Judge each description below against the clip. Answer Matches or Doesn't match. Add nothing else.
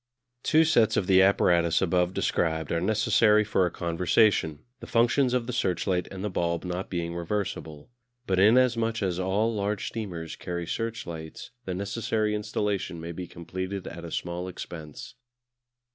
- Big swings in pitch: Doesn't match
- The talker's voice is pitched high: Doesn't match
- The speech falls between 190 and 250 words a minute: Doesn't match